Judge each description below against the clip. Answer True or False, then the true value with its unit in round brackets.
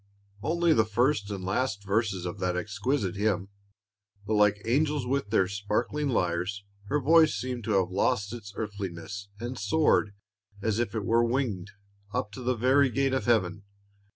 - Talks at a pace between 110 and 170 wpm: True (165 wpm)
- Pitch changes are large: False (4.3 semitones)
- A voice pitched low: True (110 Hz)